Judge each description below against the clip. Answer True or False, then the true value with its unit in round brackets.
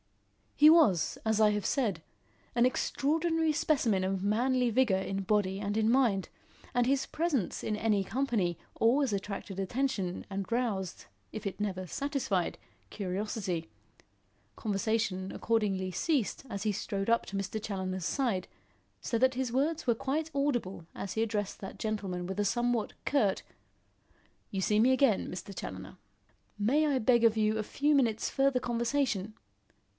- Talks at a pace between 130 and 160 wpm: True (150 wpm)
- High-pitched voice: True (220 Hz)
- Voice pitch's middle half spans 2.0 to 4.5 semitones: False (4.9 semitones)